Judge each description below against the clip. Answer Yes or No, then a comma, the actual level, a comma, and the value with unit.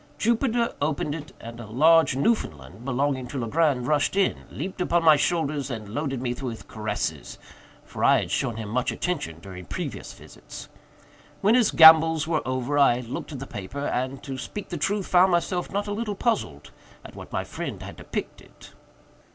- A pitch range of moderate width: No, wide, 5.9 semitones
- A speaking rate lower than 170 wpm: No, average, 180 wpm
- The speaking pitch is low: No, medium, 145 Hz